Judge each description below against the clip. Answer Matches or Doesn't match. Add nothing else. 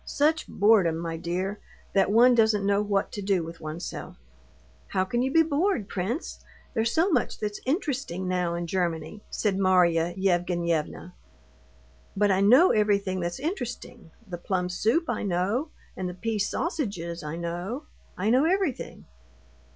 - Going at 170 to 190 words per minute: Doesn't match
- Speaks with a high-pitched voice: Matches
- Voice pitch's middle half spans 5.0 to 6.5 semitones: Matches